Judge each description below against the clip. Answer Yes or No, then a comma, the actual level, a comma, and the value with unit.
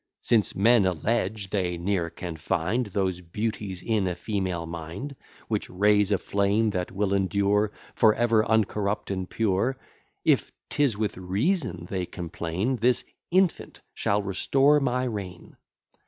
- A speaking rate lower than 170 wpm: Yes, average, 140 wpm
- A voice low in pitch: Yes, low, 100 Hz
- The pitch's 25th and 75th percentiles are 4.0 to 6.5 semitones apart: No, average, 3.4 semitones